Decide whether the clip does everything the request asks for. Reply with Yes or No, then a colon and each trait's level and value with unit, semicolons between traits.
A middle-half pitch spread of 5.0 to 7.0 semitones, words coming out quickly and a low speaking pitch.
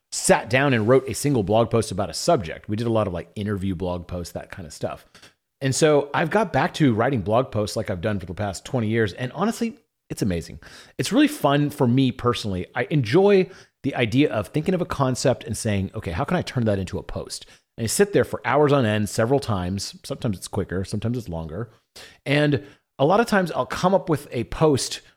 Yes: wide, 5.5 semitones; fast, 235 wpm; low, 120 Hz